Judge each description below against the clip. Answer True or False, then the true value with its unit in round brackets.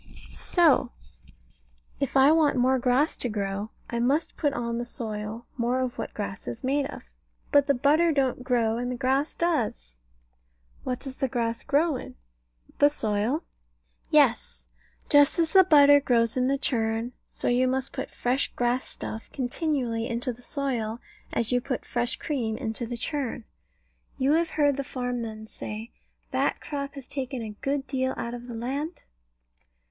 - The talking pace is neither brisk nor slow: True (170 wpm)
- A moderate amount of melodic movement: True (3.3 semitones)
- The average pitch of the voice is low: False (255 Hz)